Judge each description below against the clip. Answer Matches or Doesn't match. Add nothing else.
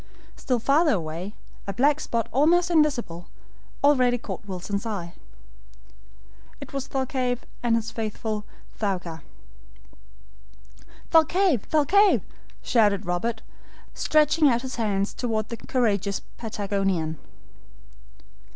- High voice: Matches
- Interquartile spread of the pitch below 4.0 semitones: Doesn't match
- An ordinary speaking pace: Doesn't match